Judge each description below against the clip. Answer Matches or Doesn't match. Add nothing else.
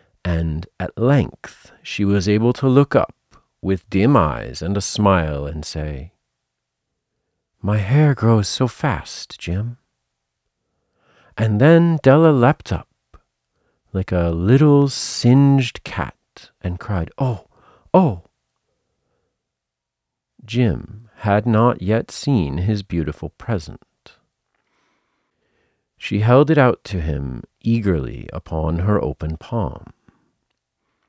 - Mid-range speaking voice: Doesn't match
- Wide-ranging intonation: Matches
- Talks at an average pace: Doesn't match